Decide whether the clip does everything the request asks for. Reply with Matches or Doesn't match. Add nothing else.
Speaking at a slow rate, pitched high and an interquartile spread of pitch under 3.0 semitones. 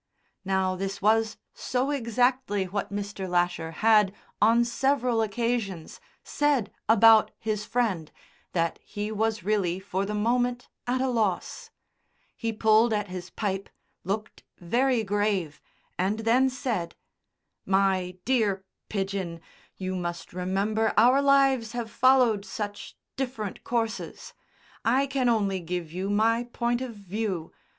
Doesn't match